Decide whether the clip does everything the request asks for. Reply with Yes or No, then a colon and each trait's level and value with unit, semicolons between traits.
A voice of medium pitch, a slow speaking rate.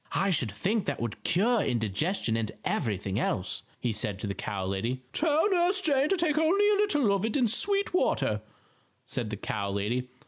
No: medium, 175 Hz; average, 195 wpm